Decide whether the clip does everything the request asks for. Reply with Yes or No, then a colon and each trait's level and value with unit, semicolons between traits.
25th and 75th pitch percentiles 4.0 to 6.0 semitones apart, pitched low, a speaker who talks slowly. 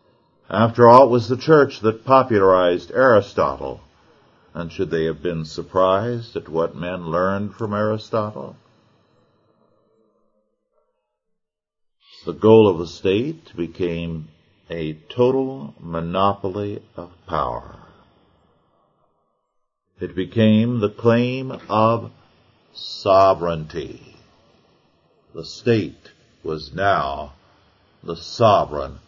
Yes: average, 4.7 semitones; low, 100 Hz; slow, 90 wpm